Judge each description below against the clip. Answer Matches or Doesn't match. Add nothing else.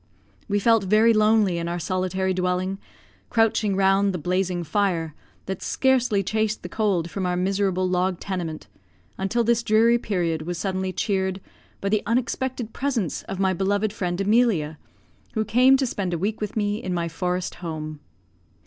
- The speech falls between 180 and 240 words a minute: Doesn't match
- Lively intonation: Doesn't match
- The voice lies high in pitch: Matches